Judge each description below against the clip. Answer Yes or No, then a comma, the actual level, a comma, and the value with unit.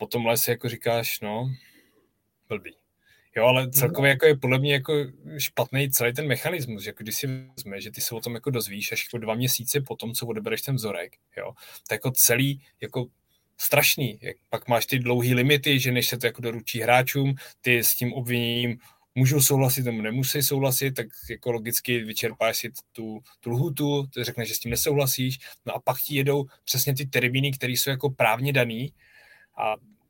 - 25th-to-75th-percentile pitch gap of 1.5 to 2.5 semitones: No, average, 2.9 semitones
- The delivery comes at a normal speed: No, fast, 195 wpm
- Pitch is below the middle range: Yes, low, 125 Hz